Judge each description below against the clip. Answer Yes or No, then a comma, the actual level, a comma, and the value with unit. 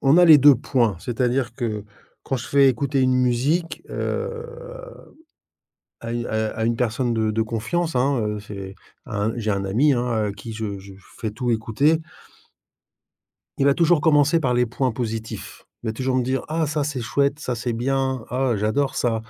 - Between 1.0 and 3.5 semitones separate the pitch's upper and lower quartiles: No, average, 3.9 semitones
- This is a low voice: Yes, low, 125 Hz